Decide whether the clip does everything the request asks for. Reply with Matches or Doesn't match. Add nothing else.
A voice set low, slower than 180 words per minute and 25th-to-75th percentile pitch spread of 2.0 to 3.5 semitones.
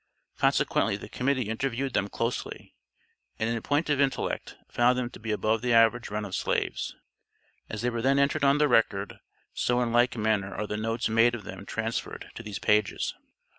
Doesn't match